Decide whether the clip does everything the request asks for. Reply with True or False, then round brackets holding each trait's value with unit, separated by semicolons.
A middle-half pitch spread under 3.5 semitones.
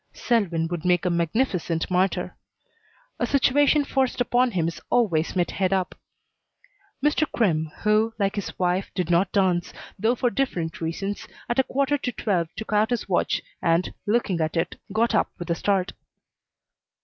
False (5.5 semitones)